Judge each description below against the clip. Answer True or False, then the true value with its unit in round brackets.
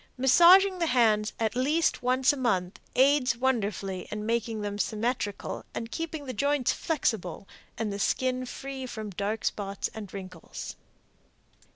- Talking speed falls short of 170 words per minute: True (145 wpm)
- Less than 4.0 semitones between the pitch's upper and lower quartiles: False (4.3 semitones)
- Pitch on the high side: True (235 Hz)